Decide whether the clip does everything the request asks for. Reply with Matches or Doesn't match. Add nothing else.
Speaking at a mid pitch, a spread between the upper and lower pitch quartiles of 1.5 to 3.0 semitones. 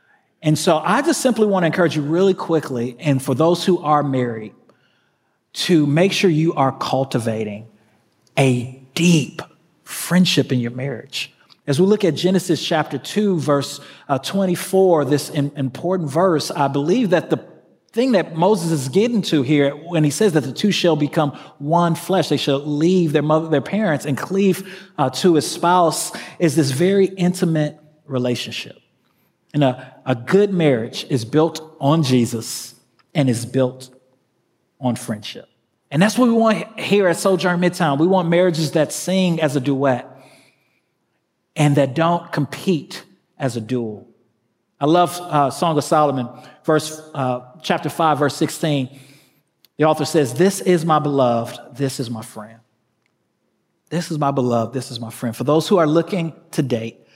Doesn't match